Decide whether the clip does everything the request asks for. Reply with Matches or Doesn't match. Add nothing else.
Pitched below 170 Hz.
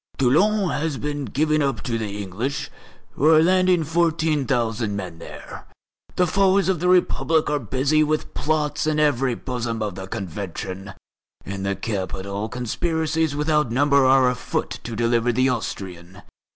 Matches